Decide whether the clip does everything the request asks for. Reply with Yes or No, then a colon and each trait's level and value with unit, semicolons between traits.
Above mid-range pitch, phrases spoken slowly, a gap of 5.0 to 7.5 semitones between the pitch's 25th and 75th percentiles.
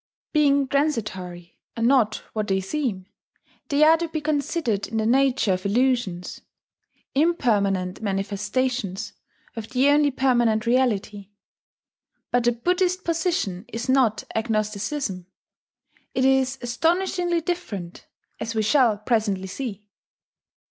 Yes: high, 240 Hz; slow, 115 wpm; wide, 5.5 semitones